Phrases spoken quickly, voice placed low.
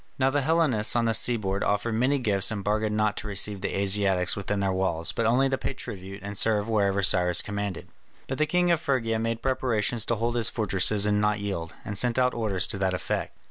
Yes: fast, 220 wpm; low, 105 Hz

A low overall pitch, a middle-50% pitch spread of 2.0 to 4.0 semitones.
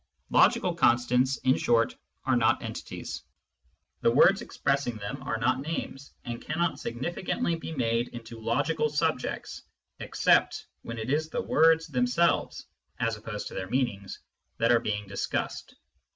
No: low, 125 Hz; average, 4.8 semitones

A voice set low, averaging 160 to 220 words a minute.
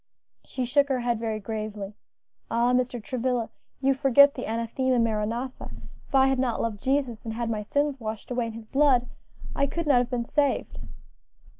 No: high, 245 Hz; average, 180 wpm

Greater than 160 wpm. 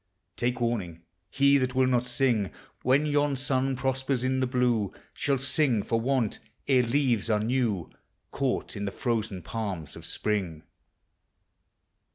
No: average, 145 wpm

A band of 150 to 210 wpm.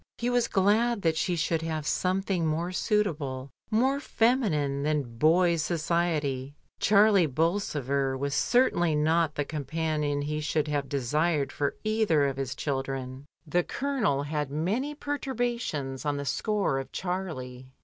No: average, 140 wpm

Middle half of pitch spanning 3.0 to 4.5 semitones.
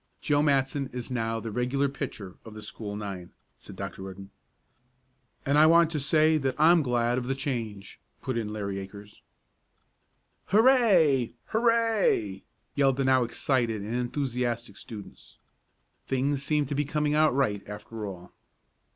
No: wide, 5.5 semitones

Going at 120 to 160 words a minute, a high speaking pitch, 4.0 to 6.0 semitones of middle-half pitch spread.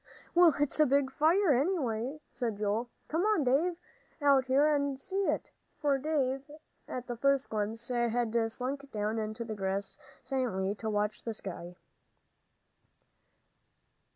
Yes: average, 140 wpm; very high, 255 Hz; average, 4.7 semitones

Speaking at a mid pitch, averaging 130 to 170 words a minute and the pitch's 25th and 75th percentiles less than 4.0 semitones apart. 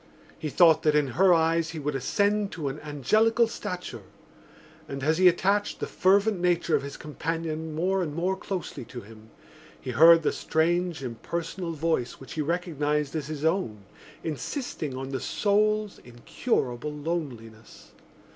No: medium, 160 Hz; average, 155 wpm; average, 4.3 semitones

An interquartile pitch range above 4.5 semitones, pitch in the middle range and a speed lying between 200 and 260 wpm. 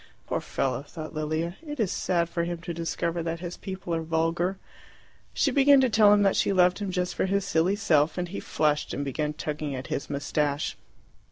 No: average, 3.7 semitones; medium, 170 Hz; fast, 205 wpm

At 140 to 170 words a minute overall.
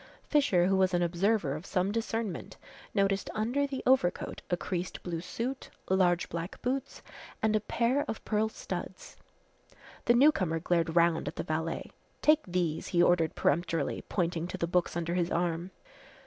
Yes: average, 160 wpm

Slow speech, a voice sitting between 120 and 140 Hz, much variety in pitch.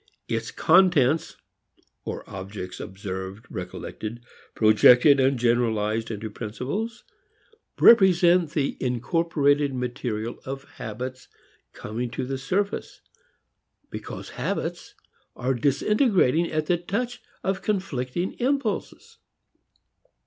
Yes: slow, 90 wpm; low, 135 Hz; wide, 7.2 semitones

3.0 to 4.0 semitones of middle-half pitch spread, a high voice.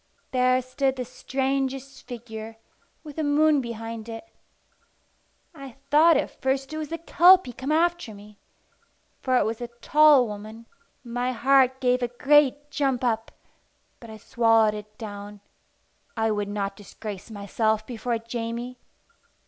Yes: average, 3.6 semitones; high, 245 Hz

